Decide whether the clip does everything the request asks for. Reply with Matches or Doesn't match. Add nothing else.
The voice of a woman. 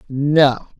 Matches